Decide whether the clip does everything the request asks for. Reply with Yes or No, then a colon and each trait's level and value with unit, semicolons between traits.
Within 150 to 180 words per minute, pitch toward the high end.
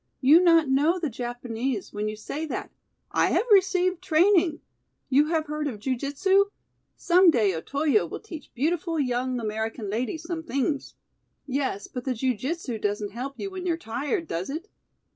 Yes: average, 170 wpm; very high, 280 Hz